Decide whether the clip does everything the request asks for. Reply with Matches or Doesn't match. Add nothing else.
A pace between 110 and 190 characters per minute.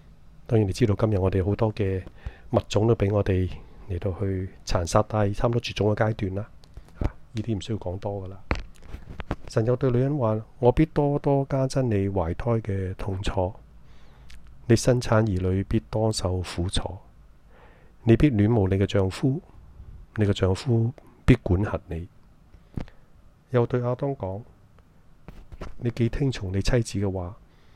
Doesn't match